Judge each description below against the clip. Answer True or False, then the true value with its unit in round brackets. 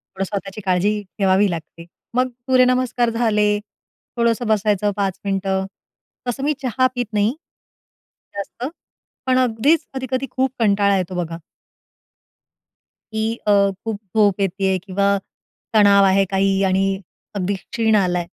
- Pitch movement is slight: False (3.3 semitones)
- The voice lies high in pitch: True (205 Hz)